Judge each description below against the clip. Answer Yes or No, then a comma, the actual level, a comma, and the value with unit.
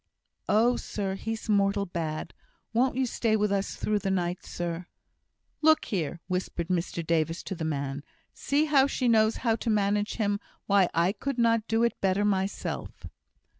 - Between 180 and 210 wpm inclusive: No, average, 170 wpm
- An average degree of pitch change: Yes, average, 4.3 semitones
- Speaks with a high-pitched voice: Yes, high, 200 Hz